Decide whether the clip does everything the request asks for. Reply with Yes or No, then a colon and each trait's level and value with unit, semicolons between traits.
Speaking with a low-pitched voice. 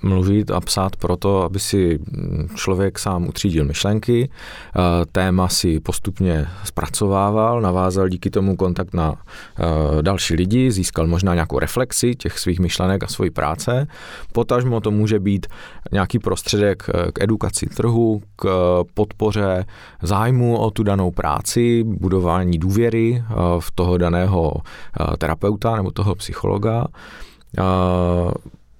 Yes: very low, 95 Hz